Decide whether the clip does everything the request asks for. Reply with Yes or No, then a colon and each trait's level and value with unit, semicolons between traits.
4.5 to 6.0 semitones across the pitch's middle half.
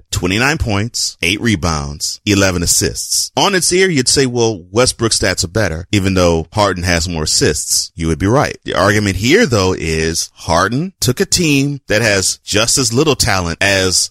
Yes: average, 4.9 semitones